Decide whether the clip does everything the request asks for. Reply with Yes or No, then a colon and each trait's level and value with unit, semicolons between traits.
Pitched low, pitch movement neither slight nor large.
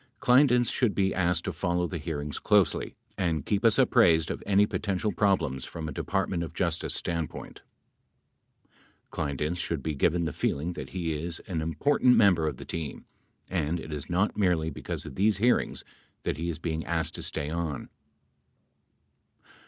Yes: very low, 85 Hz; average, 3.6 semitones